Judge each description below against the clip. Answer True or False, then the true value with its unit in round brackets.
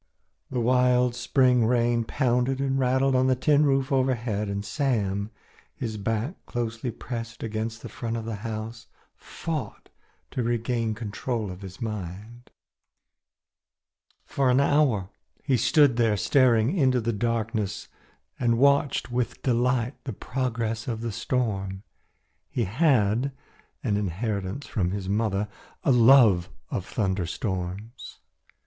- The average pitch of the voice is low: True (115 Hz)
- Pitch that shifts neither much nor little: True (3.2 semitones)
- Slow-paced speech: True (130 wpm)